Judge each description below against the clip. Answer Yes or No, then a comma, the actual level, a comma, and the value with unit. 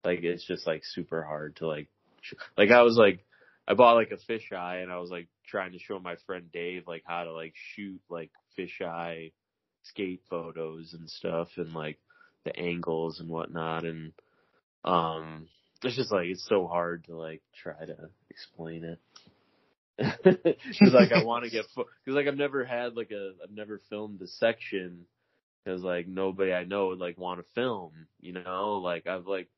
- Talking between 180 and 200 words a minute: Yes, average, 190 wpm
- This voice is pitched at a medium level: No, very low, 90 Hz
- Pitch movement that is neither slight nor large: Yes, average, 3.6 semitones